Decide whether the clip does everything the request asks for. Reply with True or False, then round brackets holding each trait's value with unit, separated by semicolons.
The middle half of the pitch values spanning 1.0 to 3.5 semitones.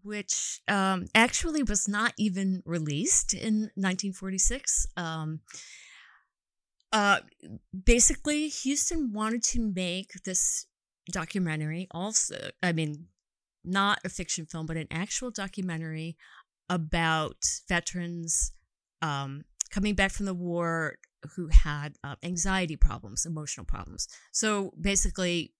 False (4.1 semitones)